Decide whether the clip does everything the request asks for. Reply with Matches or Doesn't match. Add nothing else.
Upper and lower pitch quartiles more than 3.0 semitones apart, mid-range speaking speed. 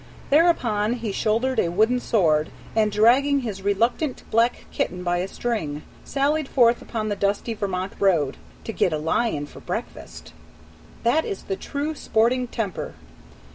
Matches